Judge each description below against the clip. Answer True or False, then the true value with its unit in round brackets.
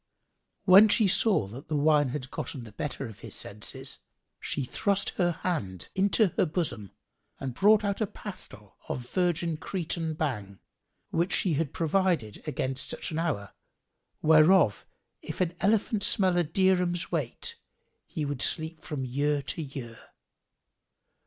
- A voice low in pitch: False (155 Hz)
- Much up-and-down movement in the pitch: True (5.7 semitones)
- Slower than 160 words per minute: True (145 wpm)